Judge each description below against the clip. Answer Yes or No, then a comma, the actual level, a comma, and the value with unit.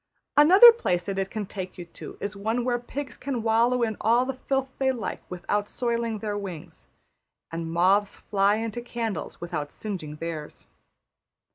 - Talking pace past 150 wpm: Yes, average, 165 wpm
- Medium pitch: No, high, 215 Hz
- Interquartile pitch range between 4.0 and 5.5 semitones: Yes, average, 4.6 semitones